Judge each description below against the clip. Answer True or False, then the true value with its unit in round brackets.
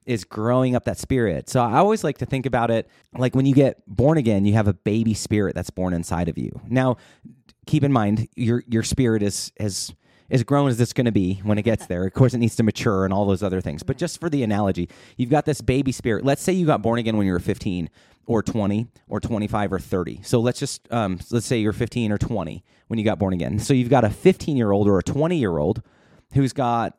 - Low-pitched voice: True (115 Hz)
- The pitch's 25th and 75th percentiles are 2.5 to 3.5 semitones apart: False (4.1 semitones)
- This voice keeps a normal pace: False (260 wpm)